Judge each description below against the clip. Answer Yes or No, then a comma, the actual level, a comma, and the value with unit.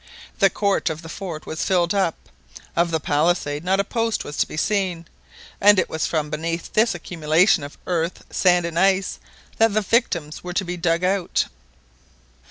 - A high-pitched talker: No, medium, 175 Hz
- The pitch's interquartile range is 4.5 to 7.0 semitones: No, average, 3.2 semitones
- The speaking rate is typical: Yes, average, 180 wpm